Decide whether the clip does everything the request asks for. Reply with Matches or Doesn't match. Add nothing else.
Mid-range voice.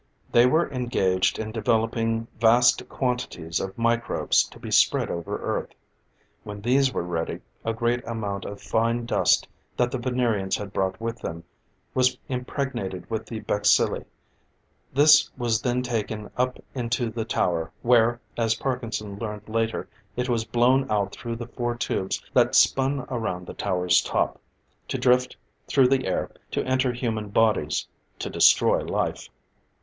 Doesn't match